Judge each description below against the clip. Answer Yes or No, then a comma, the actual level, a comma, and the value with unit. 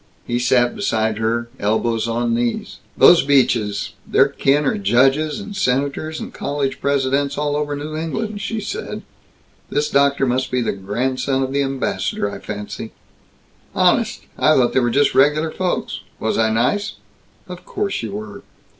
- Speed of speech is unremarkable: Yes, average, 160 wpm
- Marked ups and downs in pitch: No, average, 4.1 semitones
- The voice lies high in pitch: No, low, 135 Hz